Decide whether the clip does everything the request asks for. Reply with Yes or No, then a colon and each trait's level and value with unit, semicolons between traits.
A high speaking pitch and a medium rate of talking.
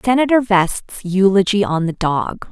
Yes: high, 200 Hz; average, 145 wpm